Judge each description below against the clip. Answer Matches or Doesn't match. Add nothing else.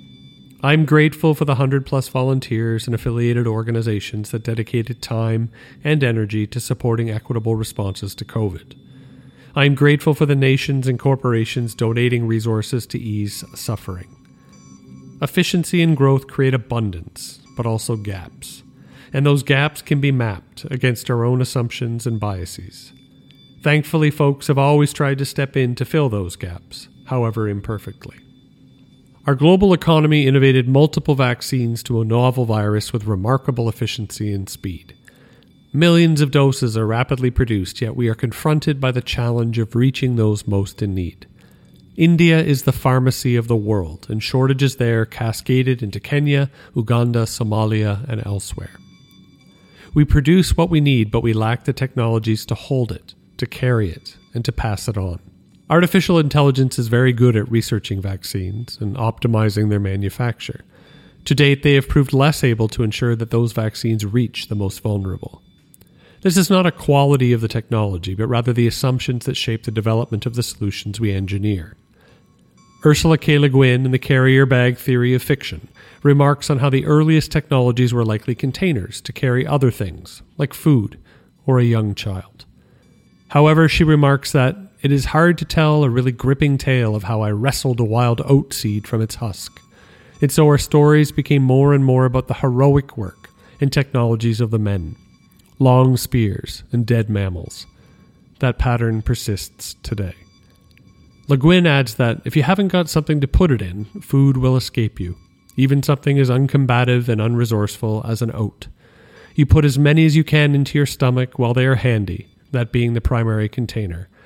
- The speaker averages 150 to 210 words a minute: Matches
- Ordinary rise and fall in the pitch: Matches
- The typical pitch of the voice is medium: Doesn't match